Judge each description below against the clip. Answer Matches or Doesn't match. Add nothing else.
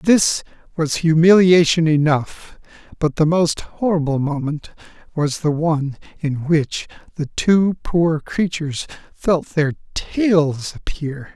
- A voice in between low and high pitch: Matches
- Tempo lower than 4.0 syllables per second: Matches